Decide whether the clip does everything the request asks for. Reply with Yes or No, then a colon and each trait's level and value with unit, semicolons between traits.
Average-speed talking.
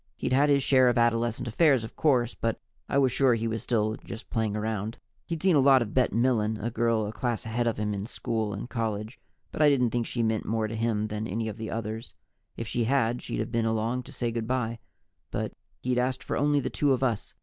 No: fast, 245 wpm